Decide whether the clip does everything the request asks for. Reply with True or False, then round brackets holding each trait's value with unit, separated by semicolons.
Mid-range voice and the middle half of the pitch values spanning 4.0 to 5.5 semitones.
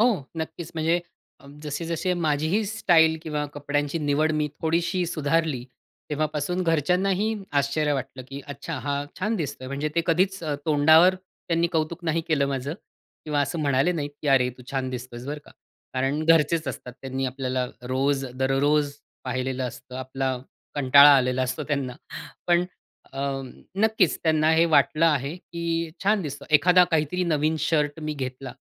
False (150 Hz; 3.4 semitones)